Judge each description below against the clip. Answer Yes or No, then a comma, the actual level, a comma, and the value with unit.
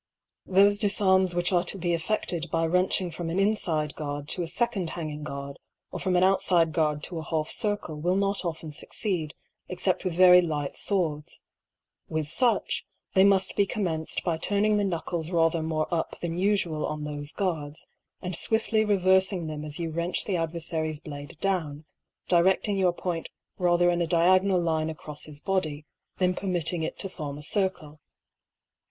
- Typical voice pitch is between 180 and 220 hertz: No, medium, 170 Hz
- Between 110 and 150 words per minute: No, average, 170 wpm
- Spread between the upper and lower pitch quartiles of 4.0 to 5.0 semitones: No, average, 3.2 semitones